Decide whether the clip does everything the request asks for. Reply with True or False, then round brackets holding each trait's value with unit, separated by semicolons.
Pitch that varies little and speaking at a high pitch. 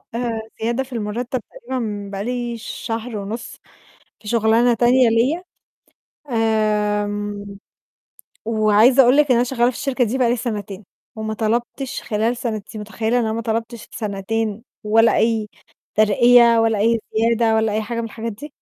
True (1.9 semitones; 225 Hz)